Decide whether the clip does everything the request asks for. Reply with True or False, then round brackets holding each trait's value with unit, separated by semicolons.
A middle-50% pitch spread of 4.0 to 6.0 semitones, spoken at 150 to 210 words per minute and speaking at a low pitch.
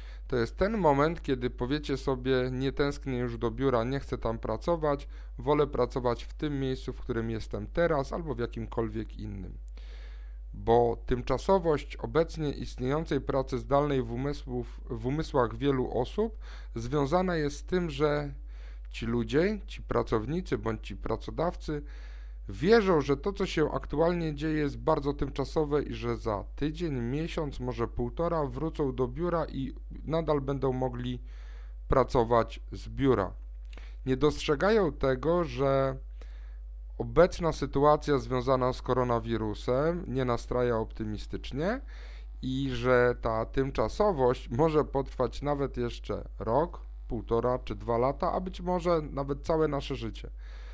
False (4.3 semitones; 130 wpm; 130 Hz)